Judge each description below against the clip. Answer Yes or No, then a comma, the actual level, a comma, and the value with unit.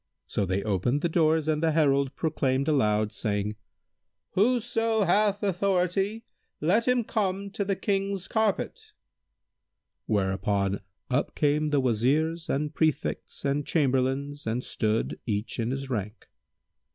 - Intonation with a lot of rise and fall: Yes, wide, 8.4 semitones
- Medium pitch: Yes, medium, 150 Hz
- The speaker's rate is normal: No, slow, 130 wpm